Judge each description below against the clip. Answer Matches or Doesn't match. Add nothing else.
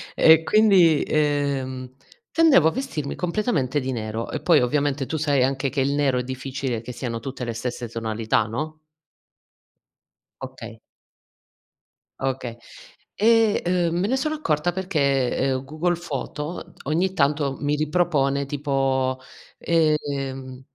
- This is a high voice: Doesn't match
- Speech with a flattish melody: Doesn't match